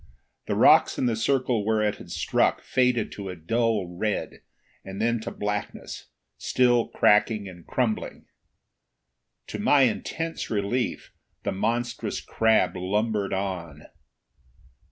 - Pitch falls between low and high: No, low, 110 Hz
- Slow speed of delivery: Yes, slow, 125 wpm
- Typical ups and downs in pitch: Yes, average, 3.2 semitones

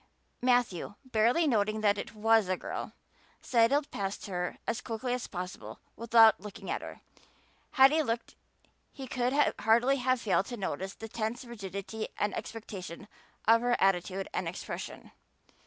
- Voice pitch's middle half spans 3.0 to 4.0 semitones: Yes, average, 3.7 semitones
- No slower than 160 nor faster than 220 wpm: No, average, 150 wpm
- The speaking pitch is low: No, high, 225 Hz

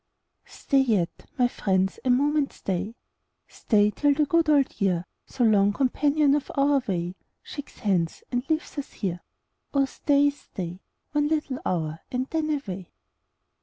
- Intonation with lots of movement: Yes, wide, 7.0 semitones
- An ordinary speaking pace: Yes, average, 160 wpm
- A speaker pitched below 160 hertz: No, very high, 255 Hz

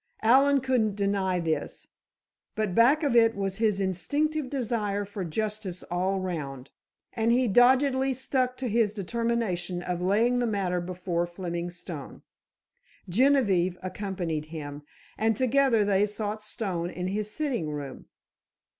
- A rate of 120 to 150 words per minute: Yes, slow, 135 wpm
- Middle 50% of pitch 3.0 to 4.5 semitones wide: No, average, 5.0 semitones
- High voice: Yes, high, 205 Hz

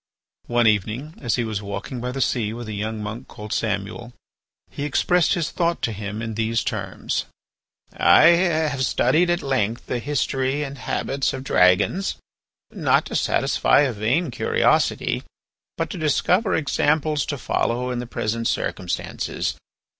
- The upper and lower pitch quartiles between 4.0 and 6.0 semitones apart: Yes, average, 5.1 semitones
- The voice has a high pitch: No, low, 125 Hz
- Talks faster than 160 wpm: No, average, 155 wpm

